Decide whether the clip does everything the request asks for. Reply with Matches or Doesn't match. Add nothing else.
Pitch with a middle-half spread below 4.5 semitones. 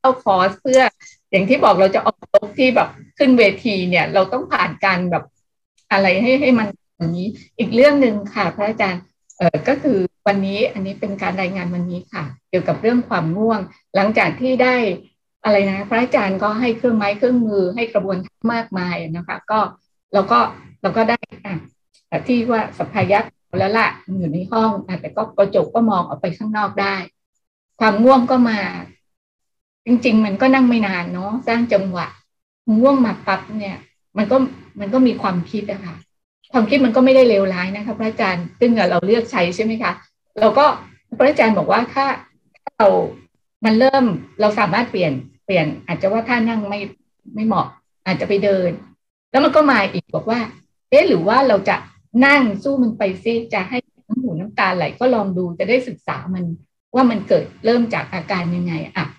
Matches